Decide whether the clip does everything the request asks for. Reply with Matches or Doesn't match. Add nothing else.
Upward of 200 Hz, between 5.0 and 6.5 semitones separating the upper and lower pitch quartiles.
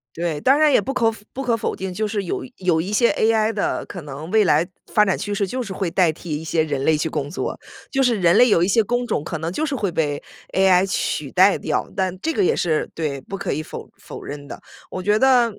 Doesn't match